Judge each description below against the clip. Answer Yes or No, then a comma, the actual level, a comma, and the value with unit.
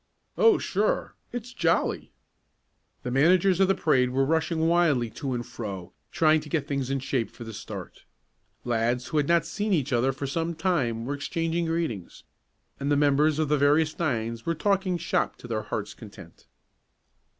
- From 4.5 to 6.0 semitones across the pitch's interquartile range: Yes, average, 5.2 semitones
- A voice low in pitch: No, medium, 145 Hz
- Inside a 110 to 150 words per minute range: No, average, 175 wpm